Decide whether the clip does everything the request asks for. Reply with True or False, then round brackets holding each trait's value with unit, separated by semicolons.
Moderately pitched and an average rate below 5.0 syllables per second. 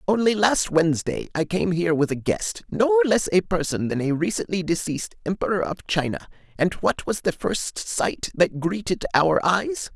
True (165 Hz; 4.8 syllables/s)